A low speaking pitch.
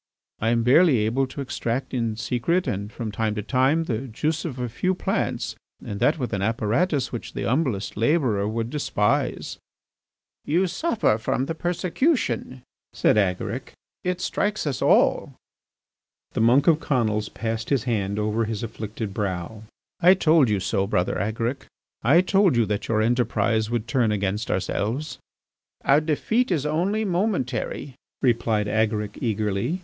Yes: low, 120 Hz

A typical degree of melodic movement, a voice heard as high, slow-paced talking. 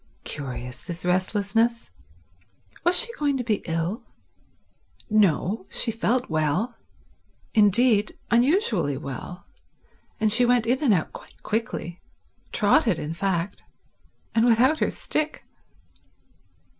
No: wide, 5.8 semitones; high, 215 Hz; slow, 105 wpm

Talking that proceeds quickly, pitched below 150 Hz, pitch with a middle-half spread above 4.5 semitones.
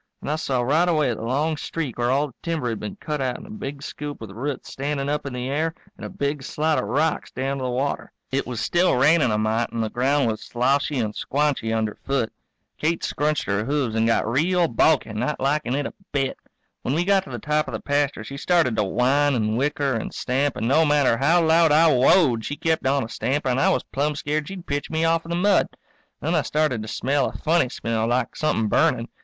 No: fast, 240 wpm; medium, 140 Hz; average, 3.8 semitones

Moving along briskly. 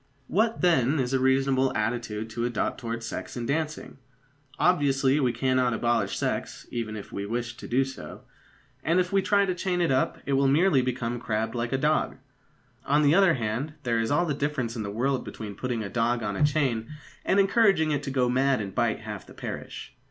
Yes: fast, 210 wpm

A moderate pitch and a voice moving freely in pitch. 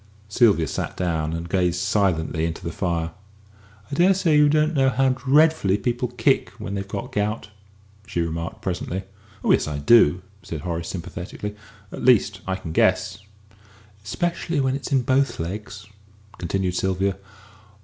No: very low, 95 Hz; wide, 6.9 semitones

